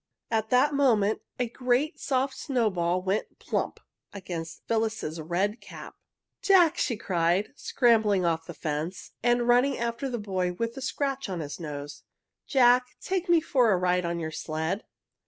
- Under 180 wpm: Yes, average, 155 wpm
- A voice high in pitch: Yes, high, 220 Hz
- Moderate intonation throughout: No, wide, 6.2 semitones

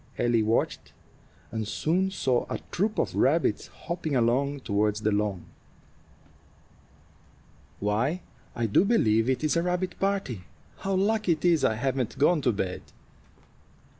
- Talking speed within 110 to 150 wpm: Yes, slow, 135 wpm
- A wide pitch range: Yes, wide, 8.3 semitones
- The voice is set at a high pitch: No, low, 130 Hz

